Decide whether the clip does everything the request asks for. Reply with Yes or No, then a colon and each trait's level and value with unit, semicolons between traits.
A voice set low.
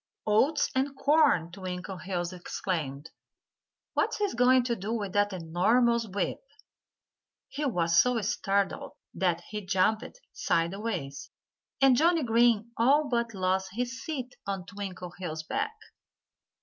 No: high, 205 Hz